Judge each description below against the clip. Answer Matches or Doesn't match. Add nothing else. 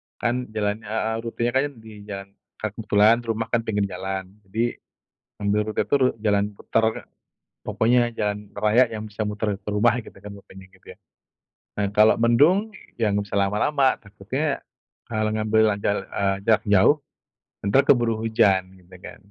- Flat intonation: Matches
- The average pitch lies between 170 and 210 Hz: Doesn't match